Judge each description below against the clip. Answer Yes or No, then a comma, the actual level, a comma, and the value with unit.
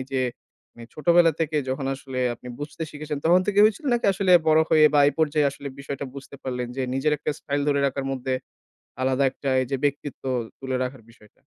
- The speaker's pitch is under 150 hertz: Yes, medium, 140 Hz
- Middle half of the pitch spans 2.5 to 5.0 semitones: Yes, average, 2.8 semitones